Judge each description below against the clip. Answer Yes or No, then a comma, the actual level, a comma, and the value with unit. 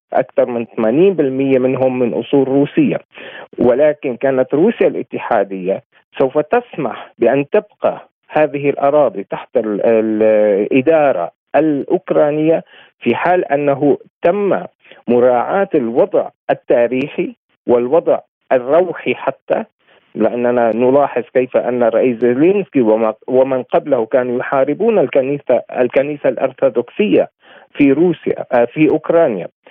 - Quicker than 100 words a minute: No, average, 95 wpm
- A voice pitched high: No, low, 135 Hz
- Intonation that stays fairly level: No, average, 3.7 semitones